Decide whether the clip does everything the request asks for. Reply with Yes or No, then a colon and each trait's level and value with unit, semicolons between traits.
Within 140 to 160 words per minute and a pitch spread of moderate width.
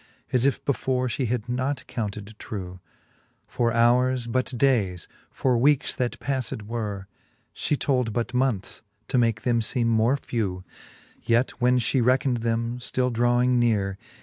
No: average, 150 wpm; narrow, 2.3 semitones